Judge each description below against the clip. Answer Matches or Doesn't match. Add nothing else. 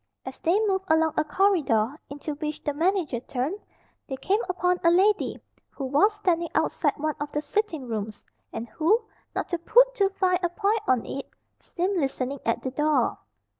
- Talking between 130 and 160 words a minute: Doesn't match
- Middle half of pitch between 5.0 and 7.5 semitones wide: Matches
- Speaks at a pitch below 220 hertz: Doesn't match